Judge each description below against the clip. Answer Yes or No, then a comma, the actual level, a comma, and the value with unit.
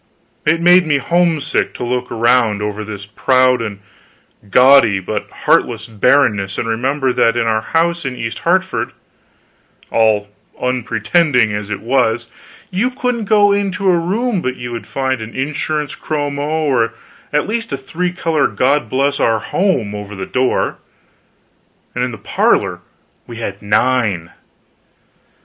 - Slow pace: No, average, 145 wpm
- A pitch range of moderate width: No, wide, 6.1 semitones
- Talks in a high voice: No, low, 130 Hz